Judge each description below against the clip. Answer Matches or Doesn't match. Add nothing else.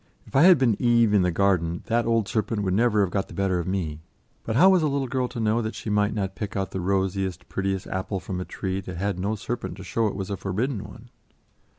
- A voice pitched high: Doesn't match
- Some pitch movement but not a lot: Matches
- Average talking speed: Doesn't match